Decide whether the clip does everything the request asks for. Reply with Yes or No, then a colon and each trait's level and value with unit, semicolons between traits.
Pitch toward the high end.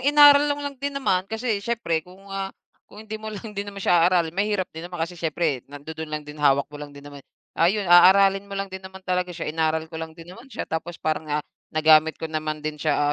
No: medium, 175 Hz